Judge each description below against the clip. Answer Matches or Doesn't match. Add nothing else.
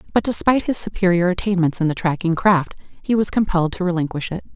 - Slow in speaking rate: Doesn't match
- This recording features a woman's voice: Matches